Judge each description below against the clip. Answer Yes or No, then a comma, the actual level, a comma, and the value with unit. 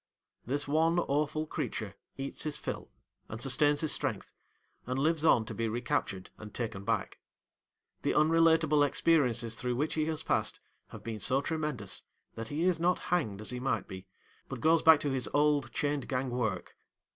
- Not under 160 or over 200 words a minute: Yes, average, 175 wpm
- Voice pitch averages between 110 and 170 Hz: Yes, medium, 140 Hz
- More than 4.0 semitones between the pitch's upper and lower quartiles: Yes, average, 4.7 semitones